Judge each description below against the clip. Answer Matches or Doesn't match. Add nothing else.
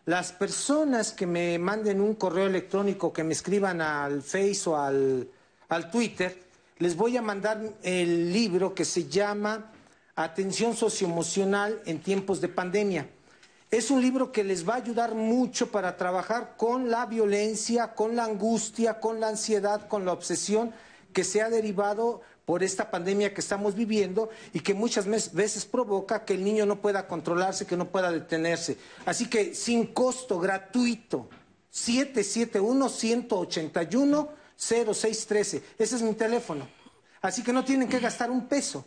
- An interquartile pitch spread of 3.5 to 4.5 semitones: Matches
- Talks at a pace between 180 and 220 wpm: Doesn't match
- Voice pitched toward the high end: Matches